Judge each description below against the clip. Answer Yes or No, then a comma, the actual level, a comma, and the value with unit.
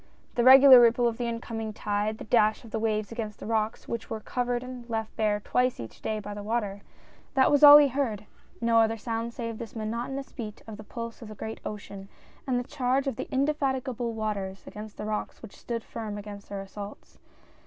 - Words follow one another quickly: Yes, fast, 215 wpm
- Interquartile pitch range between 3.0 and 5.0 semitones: No, narrow, 2.6 semitones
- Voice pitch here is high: Yes, high, 225 Hz